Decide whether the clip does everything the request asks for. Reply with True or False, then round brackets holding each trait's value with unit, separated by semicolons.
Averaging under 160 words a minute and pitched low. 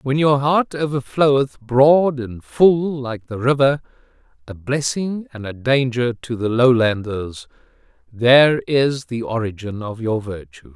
True (140 wpm; 125 Hz)